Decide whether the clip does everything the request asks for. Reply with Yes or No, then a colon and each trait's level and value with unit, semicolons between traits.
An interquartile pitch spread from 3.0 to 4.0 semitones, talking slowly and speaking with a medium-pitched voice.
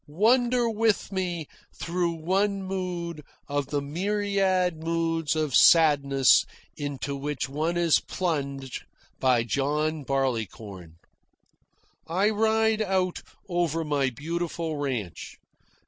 No: average, 5.0 semitones; slow, 100 wpm; medium, 165 Hz